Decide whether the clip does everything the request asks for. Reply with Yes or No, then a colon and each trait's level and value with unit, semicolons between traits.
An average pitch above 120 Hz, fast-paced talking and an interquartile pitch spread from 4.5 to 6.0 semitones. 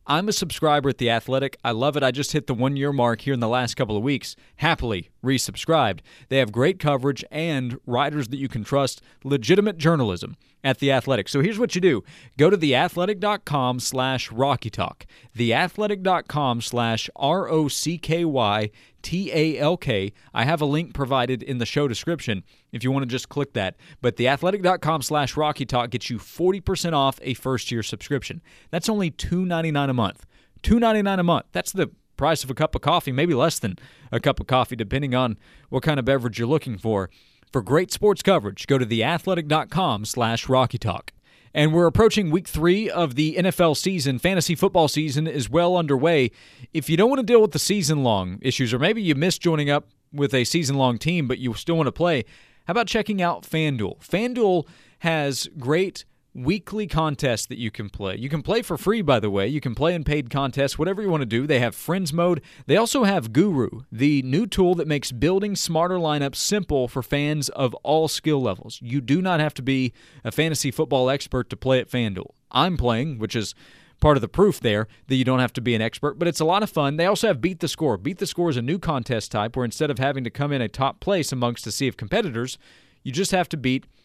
Yes: medium, 140 Hz; fast, 215 wpm; average, 5.1 semitones